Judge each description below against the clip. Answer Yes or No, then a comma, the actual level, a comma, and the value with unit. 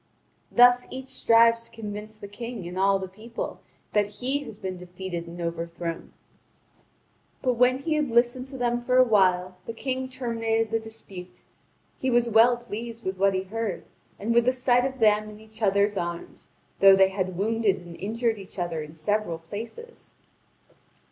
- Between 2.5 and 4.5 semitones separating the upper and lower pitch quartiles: Yes, average, 4.1 semitones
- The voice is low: No, high, 220 Hz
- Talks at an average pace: Yes, average, 175 wpm